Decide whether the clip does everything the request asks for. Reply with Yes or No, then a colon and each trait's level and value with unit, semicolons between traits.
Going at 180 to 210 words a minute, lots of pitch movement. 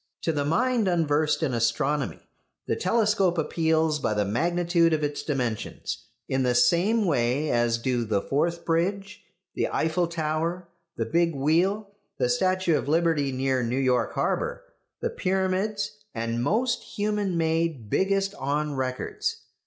No: average, 145 wpm; wide, 5.8 semitones